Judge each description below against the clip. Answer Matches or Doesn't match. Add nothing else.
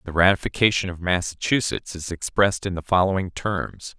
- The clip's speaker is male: Matches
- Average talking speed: Matches